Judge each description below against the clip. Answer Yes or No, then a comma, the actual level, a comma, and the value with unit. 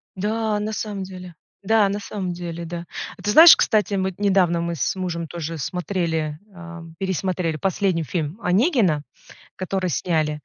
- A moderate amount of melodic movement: Yes, average, 3.0 semitones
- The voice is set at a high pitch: No, medium, 180 Hz